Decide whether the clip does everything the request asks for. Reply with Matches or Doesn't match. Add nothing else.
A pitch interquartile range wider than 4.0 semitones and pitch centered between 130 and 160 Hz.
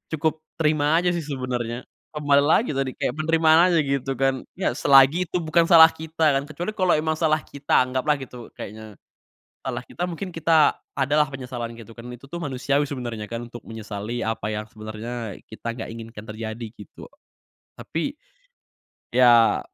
Matches